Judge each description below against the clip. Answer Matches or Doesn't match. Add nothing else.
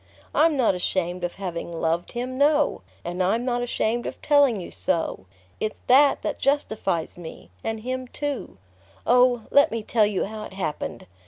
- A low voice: Doesn't match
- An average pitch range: Doesn't match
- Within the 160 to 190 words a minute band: Matches